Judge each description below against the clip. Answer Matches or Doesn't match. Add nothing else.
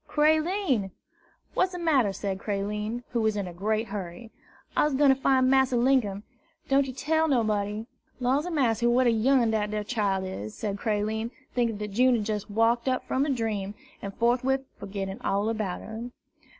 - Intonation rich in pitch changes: Doesn't match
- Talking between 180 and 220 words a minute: Matches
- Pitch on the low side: Doesn't match